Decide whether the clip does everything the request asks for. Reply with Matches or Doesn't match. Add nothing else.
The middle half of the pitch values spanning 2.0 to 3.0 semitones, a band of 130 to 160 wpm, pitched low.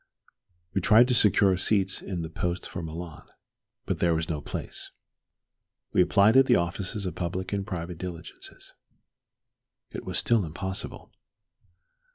Matches